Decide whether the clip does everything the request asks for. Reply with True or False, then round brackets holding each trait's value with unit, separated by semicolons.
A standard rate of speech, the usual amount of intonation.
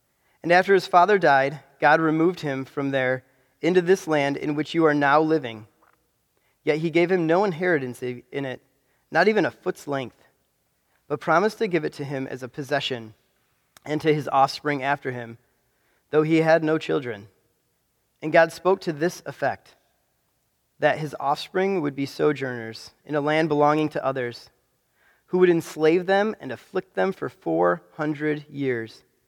True (170 wpm; 4.0 semitones)